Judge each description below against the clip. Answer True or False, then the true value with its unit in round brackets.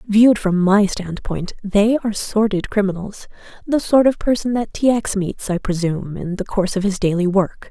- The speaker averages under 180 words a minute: False (185 wpm)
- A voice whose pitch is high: True (200 Hz)